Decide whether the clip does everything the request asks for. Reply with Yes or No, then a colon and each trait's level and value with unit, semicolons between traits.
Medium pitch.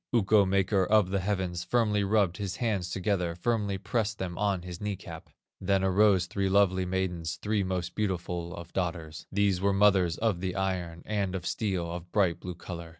No: very low, 95 Hz